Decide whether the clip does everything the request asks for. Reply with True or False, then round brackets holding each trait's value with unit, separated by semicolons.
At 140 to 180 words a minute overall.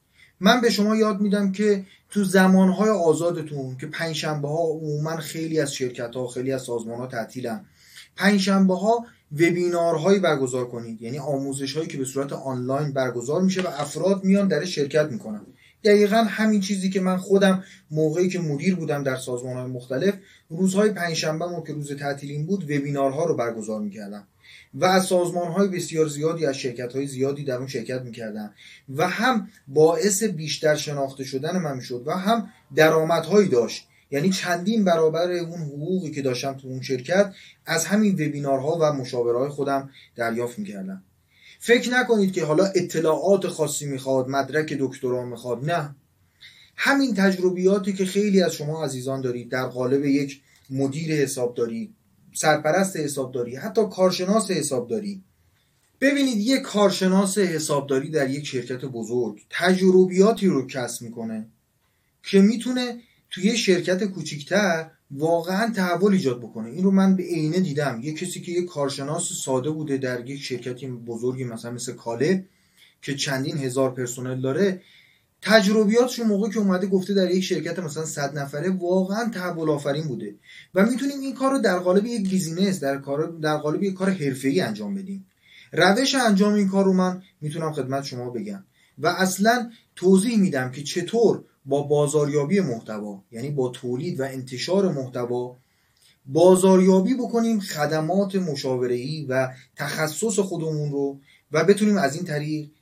True (155 wpm)